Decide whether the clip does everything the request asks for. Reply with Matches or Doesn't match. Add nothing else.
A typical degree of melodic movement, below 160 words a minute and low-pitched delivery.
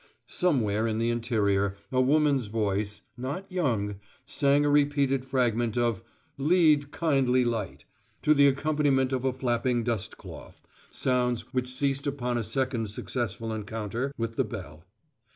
Matches